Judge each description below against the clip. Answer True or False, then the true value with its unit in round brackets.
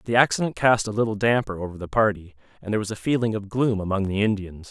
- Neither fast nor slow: False (240 wpm)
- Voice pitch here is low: True (105 Hz)